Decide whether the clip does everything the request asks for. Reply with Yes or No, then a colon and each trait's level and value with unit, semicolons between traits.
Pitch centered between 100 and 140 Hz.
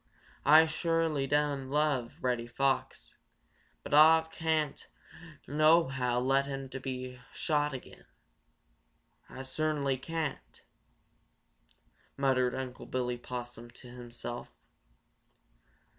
Yes: low, 135 Hz